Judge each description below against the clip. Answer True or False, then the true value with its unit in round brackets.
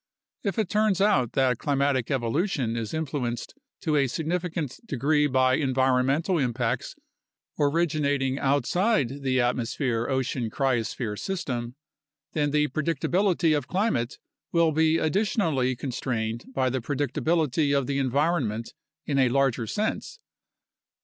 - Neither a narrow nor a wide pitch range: True (4.1 semitones)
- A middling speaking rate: False (120 wpm)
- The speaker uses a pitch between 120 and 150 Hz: True (140 Hz)